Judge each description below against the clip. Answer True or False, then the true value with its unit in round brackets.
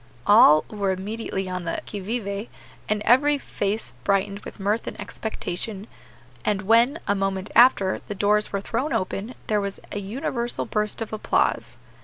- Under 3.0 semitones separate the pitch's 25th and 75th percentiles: True (2.5 semitones)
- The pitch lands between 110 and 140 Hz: False (205 Hz)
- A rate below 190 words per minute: True (160 wpm)